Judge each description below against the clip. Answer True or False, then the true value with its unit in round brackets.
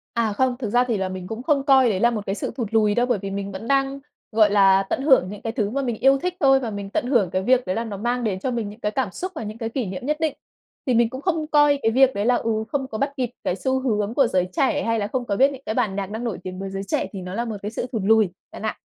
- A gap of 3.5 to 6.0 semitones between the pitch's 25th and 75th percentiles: True (4.4 semitones)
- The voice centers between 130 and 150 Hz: False (230 Hz)